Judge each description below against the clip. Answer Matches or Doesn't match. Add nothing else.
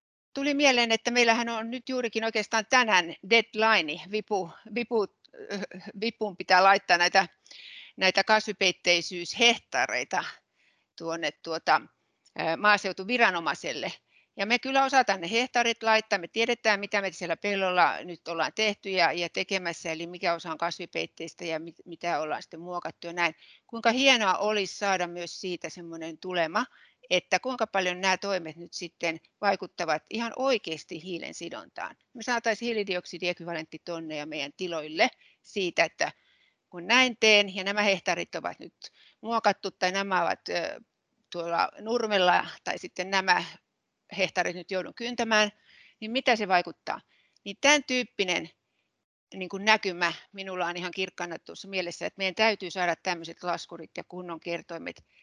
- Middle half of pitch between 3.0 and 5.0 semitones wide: Matches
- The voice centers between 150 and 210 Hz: Matches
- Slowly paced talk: Doesn't match